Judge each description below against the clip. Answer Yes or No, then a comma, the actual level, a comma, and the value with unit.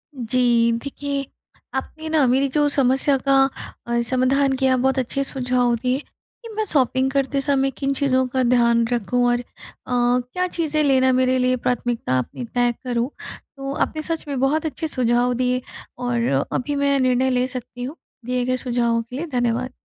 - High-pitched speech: Yes, very high, 255 Hz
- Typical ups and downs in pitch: No, narrow, 2.1 semitones